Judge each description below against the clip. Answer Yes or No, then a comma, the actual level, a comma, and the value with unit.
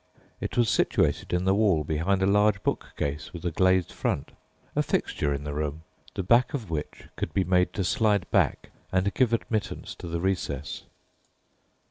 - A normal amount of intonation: Yes, average, 4.4 semitones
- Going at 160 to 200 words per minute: Yes, average, 175 wpm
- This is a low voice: Yes, very low, 95 Hz